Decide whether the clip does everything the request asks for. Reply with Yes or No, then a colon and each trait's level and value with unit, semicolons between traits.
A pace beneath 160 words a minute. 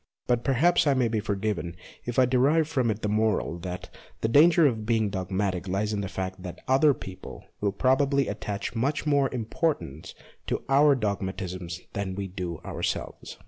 No: average, 175 wpm